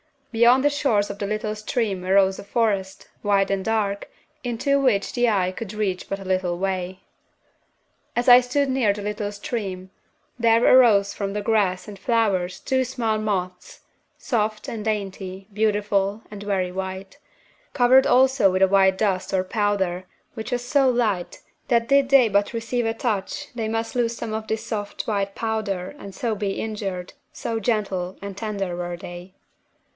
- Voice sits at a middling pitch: No, high, 205 Hz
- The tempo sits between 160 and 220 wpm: Yes, average, 170 wpm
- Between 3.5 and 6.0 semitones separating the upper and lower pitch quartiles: No, average, 3.1 semitones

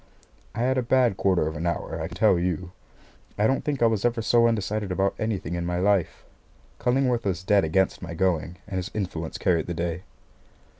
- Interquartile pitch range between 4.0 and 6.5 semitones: Yes, average, 4.7 semitones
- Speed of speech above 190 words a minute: Yes, fast, 205 wpm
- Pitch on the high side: No, very low, 95 Hz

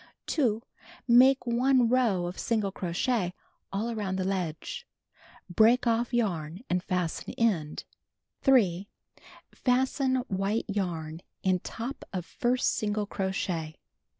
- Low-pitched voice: No, high, 205 Hz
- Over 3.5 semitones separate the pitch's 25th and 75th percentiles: Yes, average, 5.0 semitones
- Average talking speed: No, slow, 115 wpm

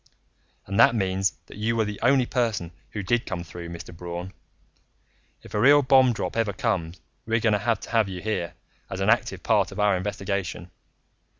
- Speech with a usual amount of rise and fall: Yes, average, 4.0 semitones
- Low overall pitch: Yes, low, 105 Hz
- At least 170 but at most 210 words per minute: Yes, average, 195 wpm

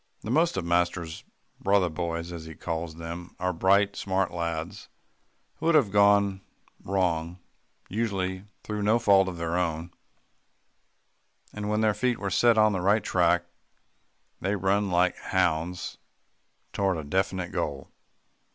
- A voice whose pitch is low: Yes, very low, 95 Hz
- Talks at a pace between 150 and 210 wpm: No, average, 140 wpm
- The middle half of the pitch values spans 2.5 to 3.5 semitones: Yes, average, 3.0 semitones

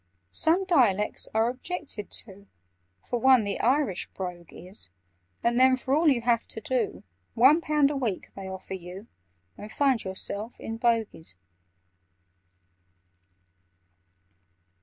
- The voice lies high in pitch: Yes, high, 230 Hz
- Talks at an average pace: No, slow, 125 wpm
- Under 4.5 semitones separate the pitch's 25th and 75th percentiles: No, average, 4.9 semitones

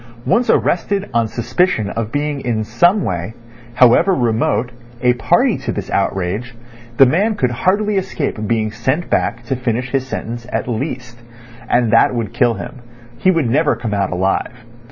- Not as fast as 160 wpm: No, average, 165 wpm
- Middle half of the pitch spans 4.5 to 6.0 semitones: Yes, average, 5.0 semitones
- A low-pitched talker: Yes, low, 120 Hz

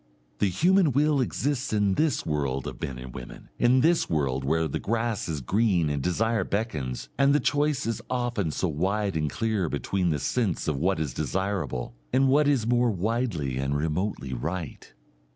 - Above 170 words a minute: Yes, average, 180 wpm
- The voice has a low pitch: Yes, very low, 95 Hz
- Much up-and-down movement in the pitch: Yes, wide, 8.3 semitones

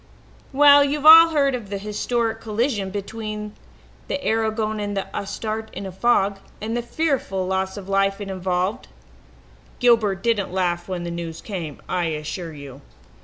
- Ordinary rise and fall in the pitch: Yes, average, 3.4 semitones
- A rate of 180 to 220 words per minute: No, average, 160 wpm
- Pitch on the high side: Yes, high, 205 Hz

